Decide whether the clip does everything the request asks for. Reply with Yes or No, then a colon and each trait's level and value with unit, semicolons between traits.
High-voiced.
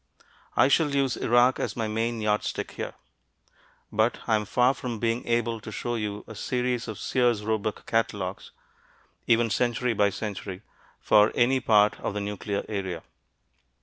No: low, 115 Hz